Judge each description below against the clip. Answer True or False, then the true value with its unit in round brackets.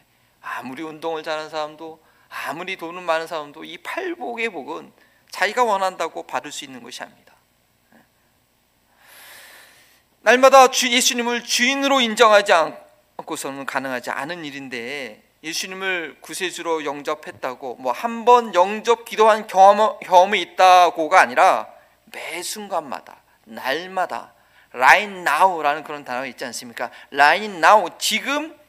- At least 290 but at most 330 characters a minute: True (305 characters per minute)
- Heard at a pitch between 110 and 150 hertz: False (180 Hz)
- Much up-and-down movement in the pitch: True (6.3 semitones)